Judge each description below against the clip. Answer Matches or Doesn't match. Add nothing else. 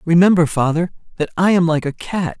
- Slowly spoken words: Doesn't match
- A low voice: Doesn't match